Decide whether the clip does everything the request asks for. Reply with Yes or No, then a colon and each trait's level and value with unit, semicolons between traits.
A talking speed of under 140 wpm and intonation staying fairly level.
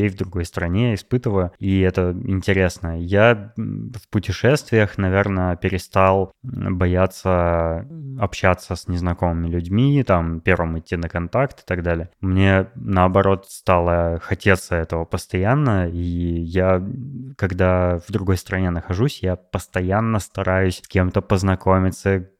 Yes: average, 120 wpm; narrow, 2.2 semitones